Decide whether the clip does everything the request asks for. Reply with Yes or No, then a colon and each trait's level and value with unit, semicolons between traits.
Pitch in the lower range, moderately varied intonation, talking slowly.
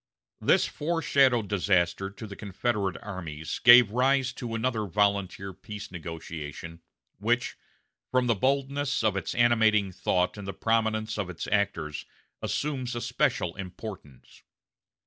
Yes: low, 105 Hz; average, 4.5 semitones; slow, 125 wpm